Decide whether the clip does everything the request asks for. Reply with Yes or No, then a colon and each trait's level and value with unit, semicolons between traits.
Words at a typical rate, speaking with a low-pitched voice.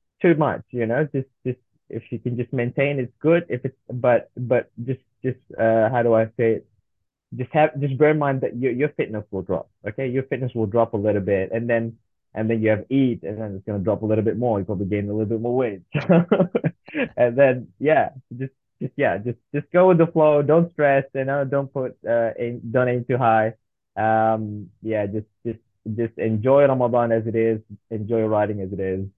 No: fast, 225 wpm; low, 120 Hz